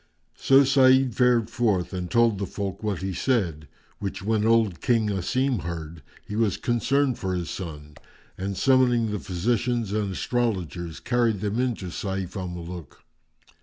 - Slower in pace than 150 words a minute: No, average, 160 wpm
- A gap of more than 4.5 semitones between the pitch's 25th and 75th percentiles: Yes, average, 4.9 semitones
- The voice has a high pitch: No, low, 105 Hz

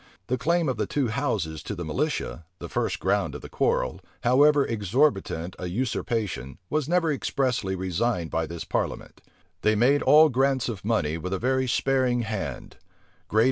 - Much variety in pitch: Yes, wide, 6.8 semitones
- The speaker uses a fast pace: No, average, 170 wpm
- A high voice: No, low, 115 Hz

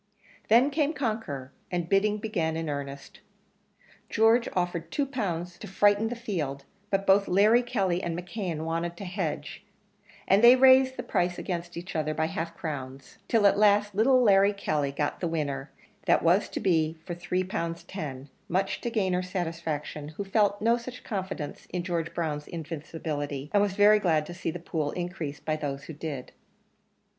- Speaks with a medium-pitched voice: Yes, medium, 175 Hz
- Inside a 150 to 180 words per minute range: Yes, average, 175 wpm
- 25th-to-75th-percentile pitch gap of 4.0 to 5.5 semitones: Yes, average, 4.5 semitones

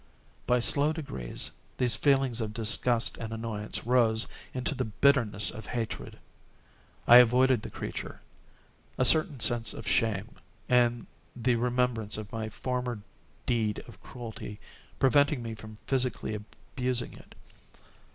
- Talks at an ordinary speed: No, slow, 130 wpm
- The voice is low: Yes, low, 120 Hz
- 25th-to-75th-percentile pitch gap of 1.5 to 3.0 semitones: Yes, narrow, 2.4 semitones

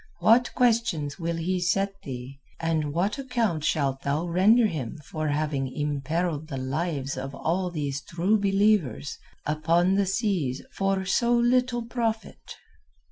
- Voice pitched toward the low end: No, medium, 170 Hz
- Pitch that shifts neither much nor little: No, wide, 5.8 semitones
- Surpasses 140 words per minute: No, slow, 135 wpm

